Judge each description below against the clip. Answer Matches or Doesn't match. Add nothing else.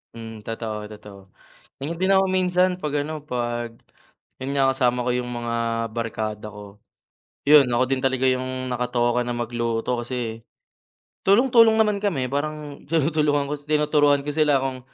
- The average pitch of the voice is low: Matches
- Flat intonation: Doesn't match